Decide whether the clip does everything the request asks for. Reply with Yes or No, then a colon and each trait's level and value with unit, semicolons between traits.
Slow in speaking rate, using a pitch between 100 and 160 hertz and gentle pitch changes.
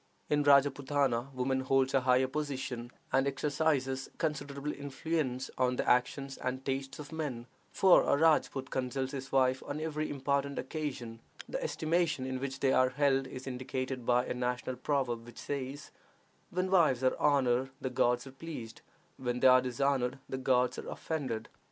No: average, 165 wpm; low, 135 Hz; narrow, 2.0 semitones